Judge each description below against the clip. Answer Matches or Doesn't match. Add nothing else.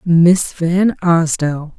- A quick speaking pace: Doesn't match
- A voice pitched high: Doesn't match